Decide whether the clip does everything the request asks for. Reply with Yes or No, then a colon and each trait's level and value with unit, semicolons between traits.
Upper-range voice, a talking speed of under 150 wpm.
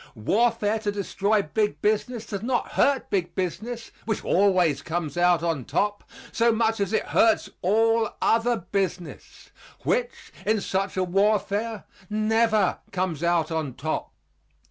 Yes: high, 205 Hz; average, 140 wpm